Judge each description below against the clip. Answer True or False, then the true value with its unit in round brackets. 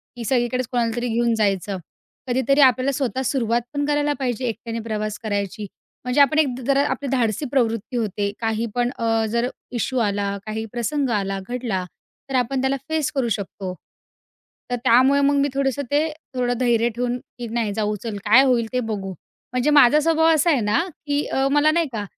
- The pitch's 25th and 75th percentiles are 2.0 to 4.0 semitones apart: True (3.6 semitones)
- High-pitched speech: True (245 Hz)